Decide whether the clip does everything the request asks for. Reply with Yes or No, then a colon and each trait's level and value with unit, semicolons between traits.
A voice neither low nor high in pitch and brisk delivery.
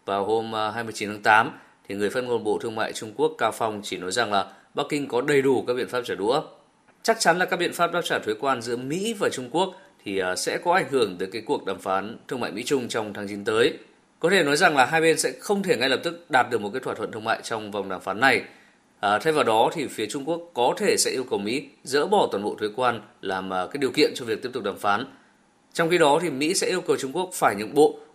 Yes: medium, 155 Hz; fast, 280 wpm